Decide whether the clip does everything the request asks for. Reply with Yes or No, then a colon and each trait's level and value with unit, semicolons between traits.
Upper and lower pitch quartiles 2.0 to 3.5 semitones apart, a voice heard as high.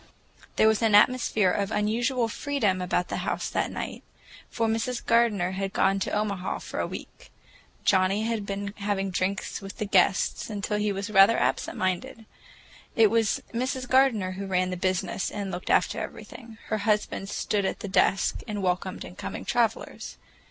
Yes: average, 2.8 semitones; high, 205 Hz